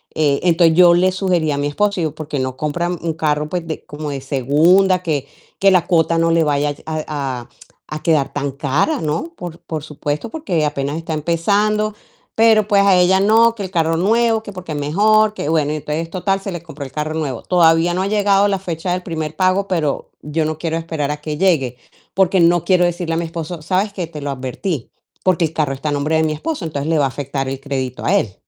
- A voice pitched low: No, medium, 165 Hz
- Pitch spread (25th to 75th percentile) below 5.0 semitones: Yes, average, 3.9 semitones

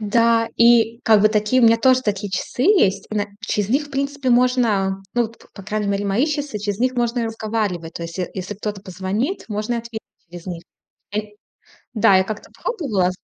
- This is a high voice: Yes, high, 215 Hz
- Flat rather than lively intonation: No, average, 3.3 semitones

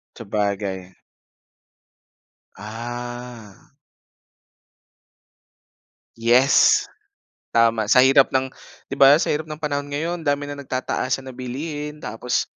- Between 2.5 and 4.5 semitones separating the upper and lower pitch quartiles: Yes, average, 3.8 semitones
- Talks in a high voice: No, low, 130 Hz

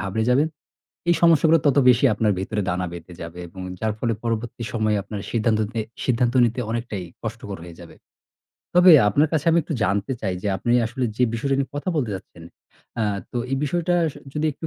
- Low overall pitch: Yes, low, 115 Hz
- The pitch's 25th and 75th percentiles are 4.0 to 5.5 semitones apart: Yes, average, 5.1 semitones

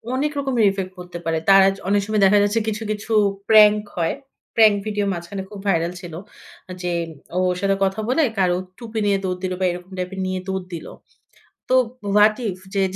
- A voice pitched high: Yes, high, 195 Hz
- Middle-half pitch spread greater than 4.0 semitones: No, narrow, 2.6 semitones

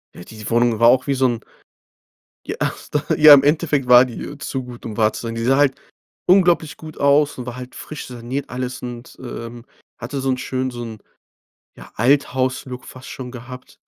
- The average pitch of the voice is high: No, low, 125 Hz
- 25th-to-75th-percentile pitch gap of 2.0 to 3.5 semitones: Yes, narrow, 2.6 semitones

